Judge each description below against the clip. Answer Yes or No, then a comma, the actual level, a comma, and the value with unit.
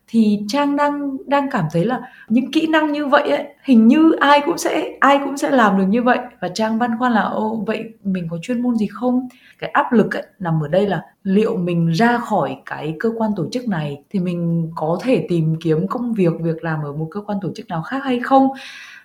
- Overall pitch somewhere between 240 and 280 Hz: No, high, 225 Hz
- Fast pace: No, average, 240 wpm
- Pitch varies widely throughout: Yes, wide, 6.8 semitones